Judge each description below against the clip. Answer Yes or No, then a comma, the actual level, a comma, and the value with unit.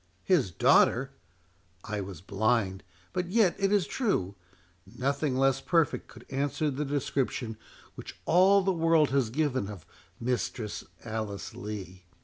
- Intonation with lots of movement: Yes, wide, 7.7 semitones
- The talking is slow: Yes, slow, 125 wpm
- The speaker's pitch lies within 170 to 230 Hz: No, low, 125 Hz